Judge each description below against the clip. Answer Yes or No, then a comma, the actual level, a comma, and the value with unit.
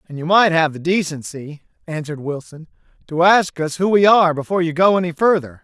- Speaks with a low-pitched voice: No, medium, 165 Hz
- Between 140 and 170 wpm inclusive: No, average, 200 wpm